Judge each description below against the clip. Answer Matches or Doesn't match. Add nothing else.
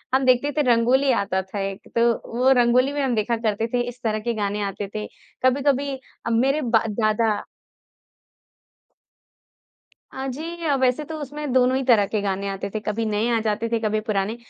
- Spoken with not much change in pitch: Doesn't match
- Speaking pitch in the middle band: Doesn't match